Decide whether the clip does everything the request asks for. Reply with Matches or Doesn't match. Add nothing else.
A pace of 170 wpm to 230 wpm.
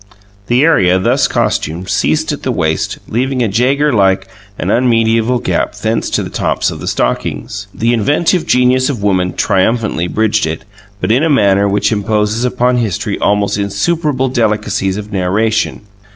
Doesn't match